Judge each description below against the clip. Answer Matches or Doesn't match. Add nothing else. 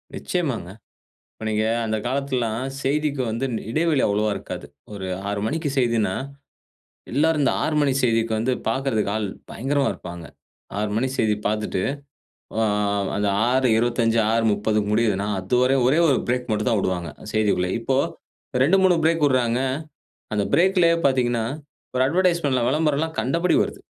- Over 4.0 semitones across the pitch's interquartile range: Matches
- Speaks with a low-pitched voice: Matches